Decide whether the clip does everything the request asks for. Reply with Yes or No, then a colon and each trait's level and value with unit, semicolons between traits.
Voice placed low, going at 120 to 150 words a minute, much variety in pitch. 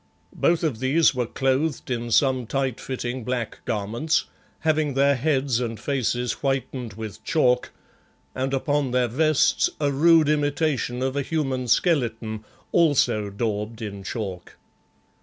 No: low, 130 Hz; slow, 135 wpm; average, 3.8 semitones